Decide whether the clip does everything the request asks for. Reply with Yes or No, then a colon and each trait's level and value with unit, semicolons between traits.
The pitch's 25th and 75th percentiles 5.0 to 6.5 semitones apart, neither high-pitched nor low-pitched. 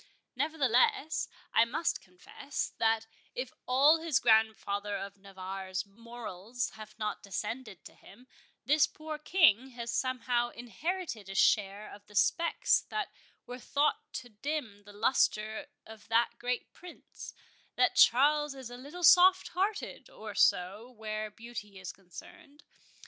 No: wide, 5.6 semitones; high, 235 Hz